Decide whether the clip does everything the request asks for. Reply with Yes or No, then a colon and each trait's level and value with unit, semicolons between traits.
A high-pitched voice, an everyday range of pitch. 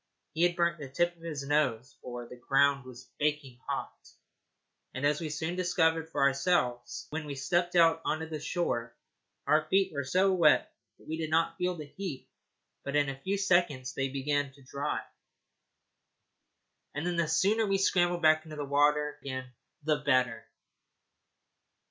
No: medium, 150 Hz; average, 3.7 semitones